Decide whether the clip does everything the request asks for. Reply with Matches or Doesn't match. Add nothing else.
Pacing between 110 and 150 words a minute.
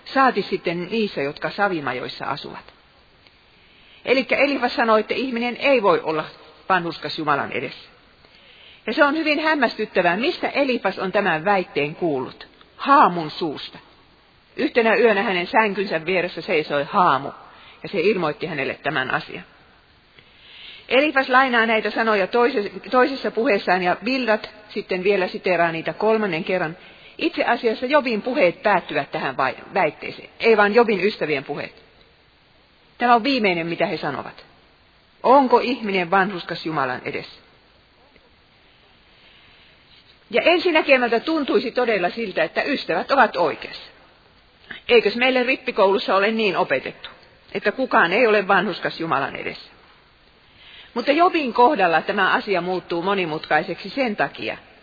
Matches